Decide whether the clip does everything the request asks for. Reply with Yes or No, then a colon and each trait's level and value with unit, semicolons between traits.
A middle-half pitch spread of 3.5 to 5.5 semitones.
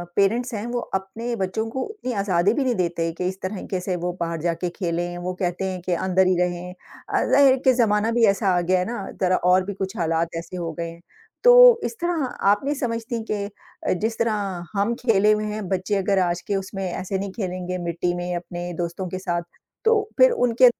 Yes: average, 4.2 semitones